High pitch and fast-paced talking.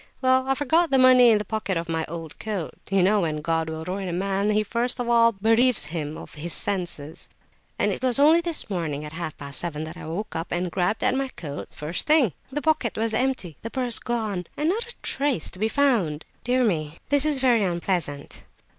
Yes: high, 205 Hz; fast, 215 wpm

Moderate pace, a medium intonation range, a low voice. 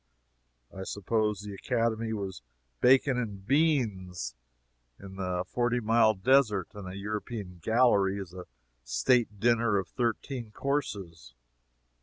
No: slow, 120 wpm; average, 3.9 semitones; low, 105 Hz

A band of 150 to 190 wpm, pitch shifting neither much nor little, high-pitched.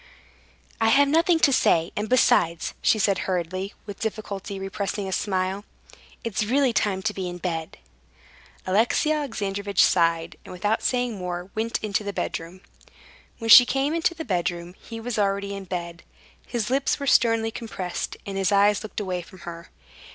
Yes: average, 165 wpm; average, 3.6 semitones; high, 200 Hz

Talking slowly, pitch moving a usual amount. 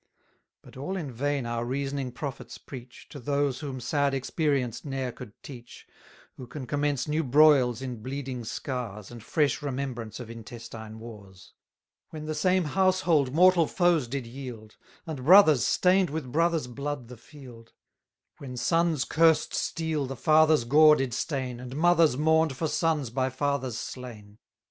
No: average, 155 wpm; average, 4.0 semitones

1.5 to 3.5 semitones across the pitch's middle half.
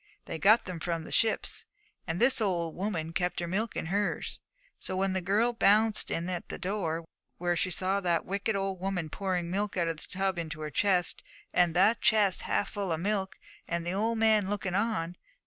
Yes: average, 3.1 semitones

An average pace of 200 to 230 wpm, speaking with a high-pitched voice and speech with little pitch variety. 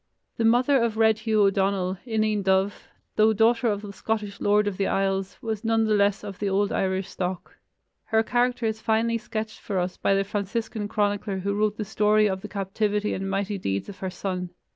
Yes: fast, 205 wpm; high, 205 Hz; narrow, 2.1 semitones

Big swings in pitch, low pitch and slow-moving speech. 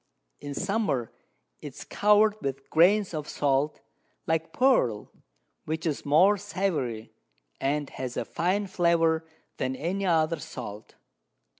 No: wide, 5.8 semitones; medium, 160 Hz; slow, 125 wpm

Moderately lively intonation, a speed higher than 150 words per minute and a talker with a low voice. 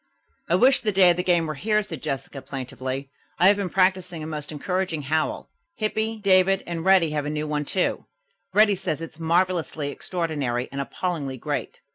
No: average, 4.2 semitones; average, 185 wpm; medium, 165 Hz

